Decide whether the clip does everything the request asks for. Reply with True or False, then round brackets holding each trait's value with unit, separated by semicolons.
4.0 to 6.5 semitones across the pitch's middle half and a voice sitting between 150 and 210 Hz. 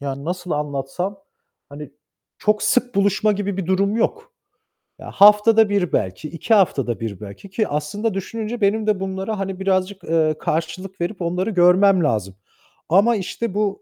True (4.6 semitones; 190 Hz)